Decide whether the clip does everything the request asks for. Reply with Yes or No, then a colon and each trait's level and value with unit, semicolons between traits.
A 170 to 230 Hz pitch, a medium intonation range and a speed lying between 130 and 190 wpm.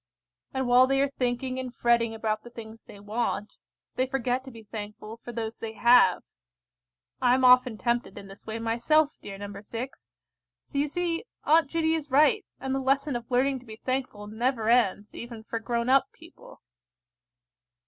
No: high, 240 Hz; average, 3.0 semitones; average, 180 wpm